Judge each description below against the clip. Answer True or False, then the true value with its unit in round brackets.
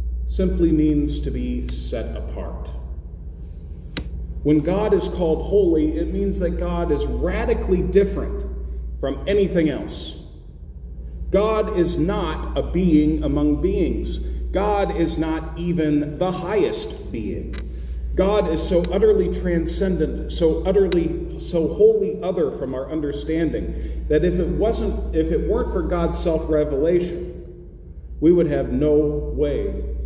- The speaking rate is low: True (125 wpm)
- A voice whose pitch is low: False (160 Hz)